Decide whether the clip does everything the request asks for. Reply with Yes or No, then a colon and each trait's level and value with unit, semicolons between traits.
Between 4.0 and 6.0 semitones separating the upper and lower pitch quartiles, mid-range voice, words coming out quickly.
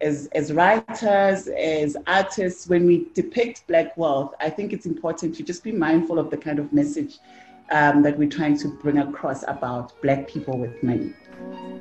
No: average, 4.7 semitones; medium, 160 Hz; average, 180 wpm